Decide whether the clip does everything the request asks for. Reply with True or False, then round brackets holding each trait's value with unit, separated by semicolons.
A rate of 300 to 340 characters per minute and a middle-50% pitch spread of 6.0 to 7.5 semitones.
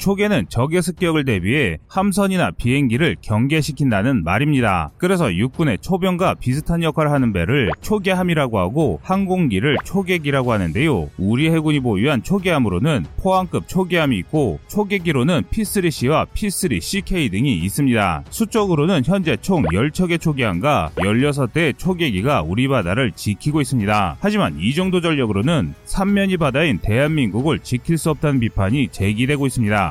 False (360 characters per minute; 7.1 semitones)